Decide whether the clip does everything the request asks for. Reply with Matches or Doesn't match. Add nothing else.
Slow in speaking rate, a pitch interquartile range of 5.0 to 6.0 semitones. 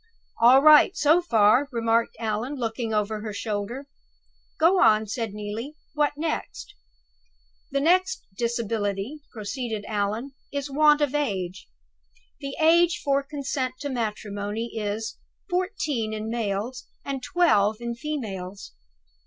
Matches